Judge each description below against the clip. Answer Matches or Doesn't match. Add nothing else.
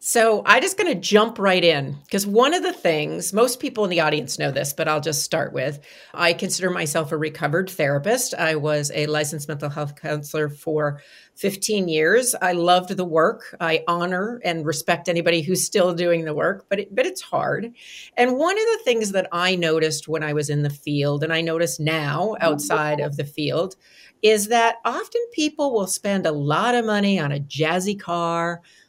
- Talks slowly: Doesn't match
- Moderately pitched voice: Matches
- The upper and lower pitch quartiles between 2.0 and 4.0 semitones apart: Doesn't match